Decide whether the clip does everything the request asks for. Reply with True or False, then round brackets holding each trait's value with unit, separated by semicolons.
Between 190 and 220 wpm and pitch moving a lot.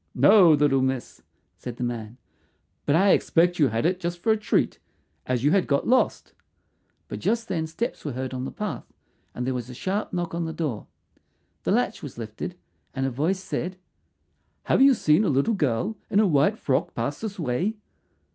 True (195 wpm; 6.8 semitones)